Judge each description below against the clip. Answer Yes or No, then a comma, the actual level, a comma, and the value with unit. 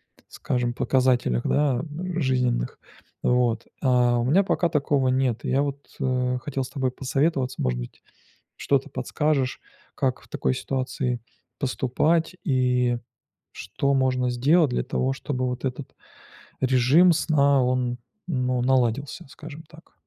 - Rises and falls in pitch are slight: Yes, narrow, 2.2 semitones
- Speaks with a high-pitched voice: No, low, 130 Hz